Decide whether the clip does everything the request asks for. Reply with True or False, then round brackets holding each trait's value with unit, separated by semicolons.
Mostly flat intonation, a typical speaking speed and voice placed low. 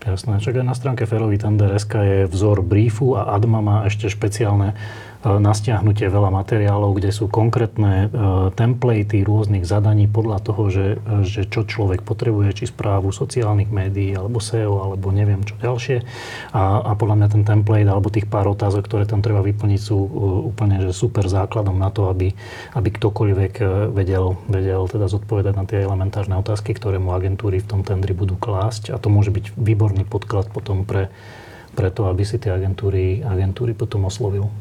False (1.9 semitones; 170 wpm; 105 Hz)